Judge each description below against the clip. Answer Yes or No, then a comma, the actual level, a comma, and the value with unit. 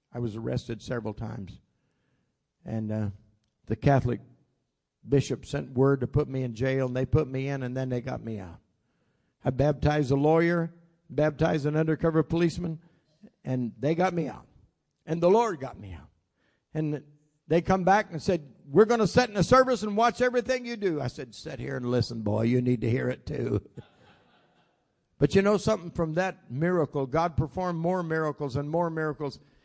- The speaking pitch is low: No, medium, 150 Hz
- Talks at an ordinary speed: Yes, average, 185 wpm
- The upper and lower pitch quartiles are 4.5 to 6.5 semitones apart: Yes, average, 5.3 semitones